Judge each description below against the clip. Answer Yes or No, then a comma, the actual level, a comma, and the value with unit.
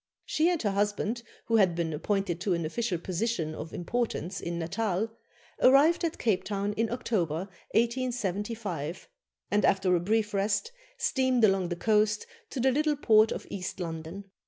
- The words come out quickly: No, average, 160 wpm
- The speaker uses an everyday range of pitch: Yes, average, 4.7 semitones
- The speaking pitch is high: Yes, high, 205 Hz